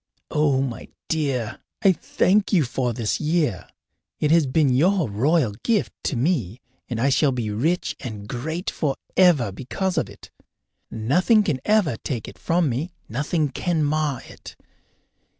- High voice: No, medium, 145 Hz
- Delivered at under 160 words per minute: Yes, average, 150 wpm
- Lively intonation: Yes, wide, 5.7 semitones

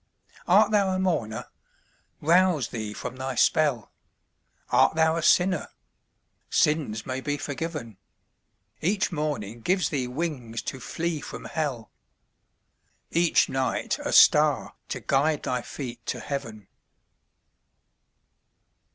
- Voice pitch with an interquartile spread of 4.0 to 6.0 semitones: Yes, wide, 5.5 semitones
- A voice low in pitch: No, medium, 145 Hz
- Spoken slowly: Yes, slow, 115 wpm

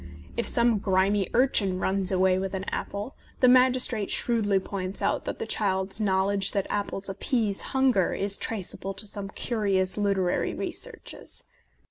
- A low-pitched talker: No, high, 200 Hz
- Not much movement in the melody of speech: No, average, 3.0 semitones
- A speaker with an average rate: Yes, average, 145 wpm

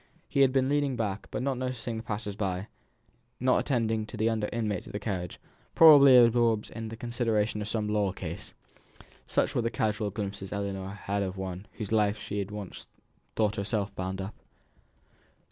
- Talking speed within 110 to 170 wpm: No, average, 180 wpm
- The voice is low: Yes, low, 105 Hz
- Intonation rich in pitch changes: No, average, 2.8 semitones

